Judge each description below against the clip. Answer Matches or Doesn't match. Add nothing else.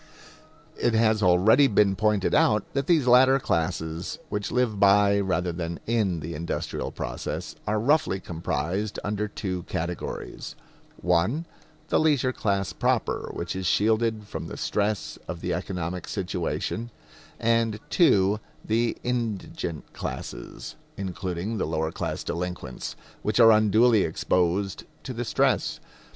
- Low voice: Matches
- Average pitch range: Matches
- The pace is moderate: Doesn't match